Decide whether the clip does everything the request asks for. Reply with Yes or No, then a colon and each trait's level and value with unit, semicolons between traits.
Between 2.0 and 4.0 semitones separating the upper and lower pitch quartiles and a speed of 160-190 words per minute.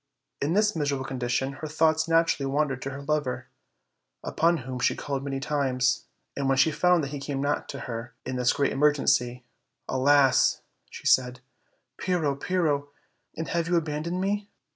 Yes: average, 3.2 semitones; average, 170 wpm